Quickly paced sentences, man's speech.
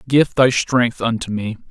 No: average, 175 wpm; male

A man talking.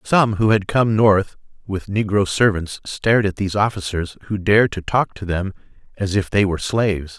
Yes: male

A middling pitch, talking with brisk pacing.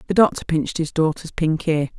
Yes: medium, 160 Hz; fast, 210 wpm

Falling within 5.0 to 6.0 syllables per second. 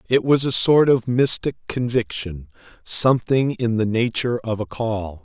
No: 4.5 syllables/s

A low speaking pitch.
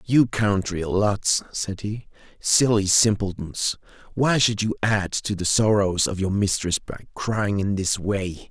Yes: low, 100 Hz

